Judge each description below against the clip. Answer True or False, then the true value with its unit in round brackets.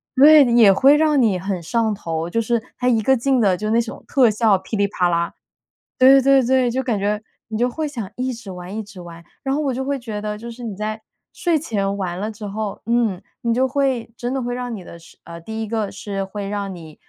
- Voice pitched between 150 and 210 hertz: False (220 Hz)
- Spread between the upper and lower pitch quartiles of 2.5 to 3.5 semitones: False (4.2 semitones)